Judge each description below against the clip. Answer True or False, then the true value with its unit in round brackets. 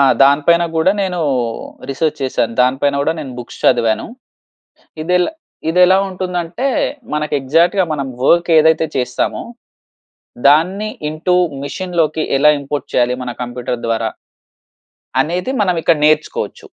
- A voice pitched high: False (155 Hz)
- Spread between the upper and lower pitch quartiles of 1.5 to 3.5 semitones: False (4.6 semitones)